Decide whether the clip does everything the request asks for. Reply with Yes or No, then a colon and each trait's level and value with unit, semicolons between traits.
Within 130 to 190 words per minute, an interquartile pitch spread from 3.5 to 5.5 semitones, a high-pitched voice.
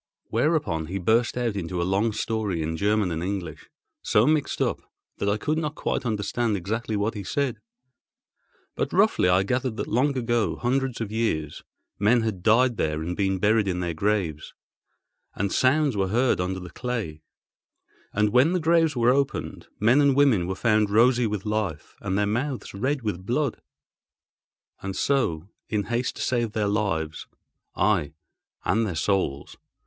No: average, 170 wpm; average, 4.6 semitones; low, 105 Hz